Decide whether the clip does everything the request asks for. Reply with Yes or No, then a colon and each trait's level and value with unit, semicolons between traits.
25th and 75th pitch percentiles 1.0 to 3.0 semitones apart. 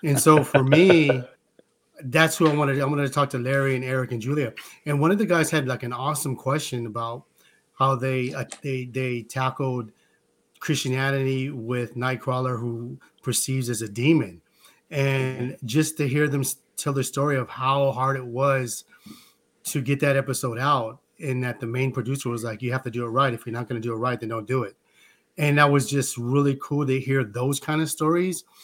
Yes: narrow, 2.4 semitones